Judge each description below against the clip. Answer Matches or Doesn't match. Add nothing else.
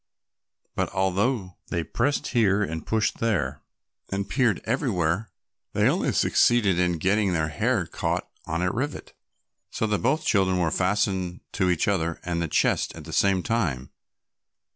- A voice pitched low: Matches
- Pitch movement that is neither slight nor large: Matches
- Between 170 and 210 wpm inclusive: Doesn't match